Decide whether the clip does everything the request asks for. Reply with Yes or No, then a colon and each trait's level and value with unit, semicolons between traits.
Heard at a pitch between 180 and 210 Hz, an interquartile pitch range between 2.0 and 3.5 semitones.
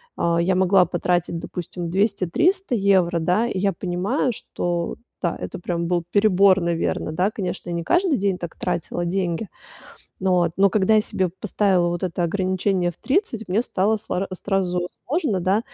Yes: medium, 185 Hz; narrow, 2.6 semitones